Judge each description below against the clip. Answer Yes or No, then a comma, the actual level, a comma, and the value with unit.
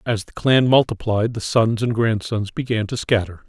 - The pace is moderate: Yes, average, 190 wpm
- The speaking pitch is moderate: No, low, 110 Hz